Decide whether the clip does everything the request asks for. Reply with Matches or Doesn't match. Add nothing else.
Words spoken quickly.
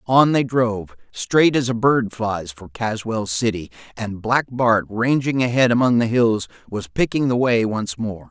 Doesn't match